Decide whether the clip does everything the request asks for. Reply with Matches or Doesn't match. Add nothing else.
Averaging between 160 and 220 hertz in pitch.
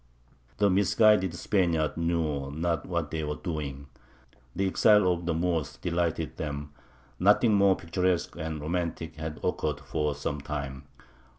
Doesn't match